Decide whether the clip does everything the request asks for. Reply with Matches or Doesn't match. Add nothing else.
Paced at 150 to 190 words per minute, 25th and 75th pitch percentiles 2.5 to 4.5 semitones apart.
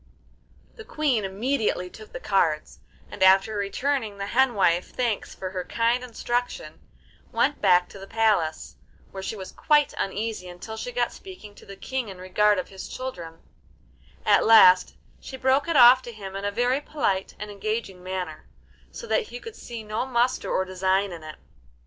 Doesn't match